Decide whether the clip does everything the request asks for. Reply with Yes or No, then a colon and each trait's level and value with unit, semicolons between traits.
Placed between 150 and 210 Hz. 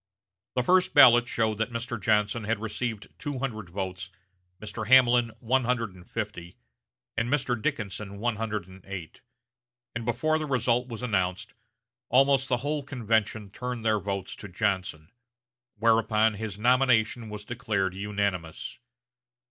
No: low, 110 Hz